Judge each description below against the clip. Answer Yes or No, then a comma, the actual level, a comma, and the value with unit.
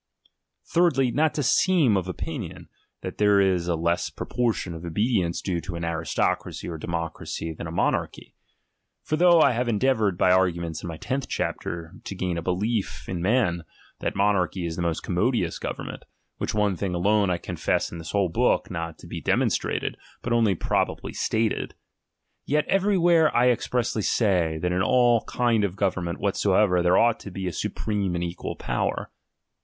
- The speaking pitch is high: No, very low, 95 Hz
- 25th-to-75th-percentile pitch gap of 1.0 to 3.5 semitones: No, wide, 5.4 semitones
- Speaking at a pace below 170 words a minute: No, average, 175 wpm